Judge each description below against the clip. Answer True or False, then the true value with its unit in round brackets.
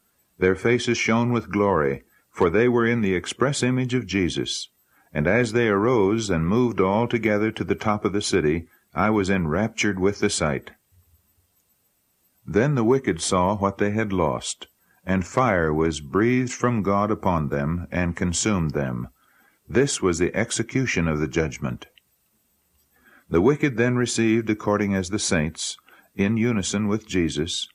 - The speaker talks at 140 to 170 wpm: True (155 wpm)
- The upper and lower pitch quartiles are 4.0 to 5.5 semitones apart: True (4.5 semitones)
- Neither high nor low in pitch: False (100 Hz)